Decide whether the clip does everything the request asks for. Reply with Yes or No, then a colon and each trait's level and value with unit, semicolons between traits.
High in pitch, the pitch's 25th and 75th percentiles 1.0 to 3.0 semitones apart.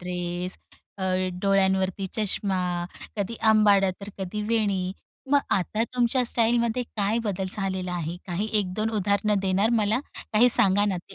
Yes: high, 200 Hz; narrow, 2.5 semitones